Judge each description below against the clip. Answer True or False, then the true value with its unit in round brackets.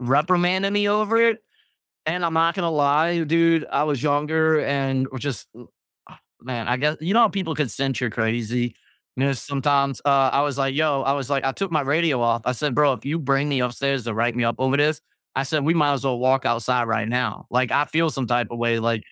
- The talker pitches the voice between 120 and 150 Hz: True (140 Hz)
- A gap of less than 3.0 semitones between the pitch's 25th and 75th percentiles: False (4.1 semitones)